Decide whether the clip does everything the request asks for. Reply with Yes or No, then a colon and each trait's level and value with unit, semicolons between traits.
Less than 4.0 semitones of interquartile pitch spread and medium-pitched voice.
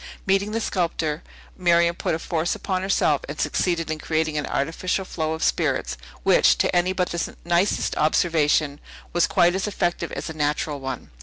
Yes: average, 2.9 semitones; medium, 170 Hz